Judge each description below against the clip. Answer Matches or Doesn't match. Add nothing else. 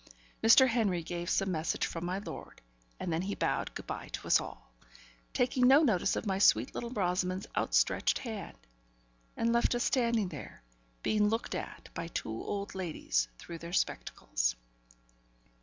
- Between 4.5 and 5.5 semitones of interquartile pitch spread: Matches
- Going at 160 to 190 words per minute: Matches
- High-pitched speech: Matches